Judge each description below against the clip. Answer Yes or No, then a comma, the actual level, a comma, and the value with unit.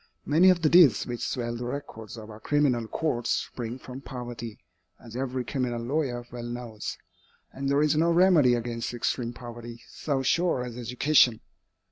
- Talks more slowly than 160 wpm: No, average, 165 wpm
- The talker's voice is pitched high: No, low, 125 Hz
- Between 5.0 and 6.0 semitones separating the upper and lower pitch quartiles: No, average, 3.4 semitones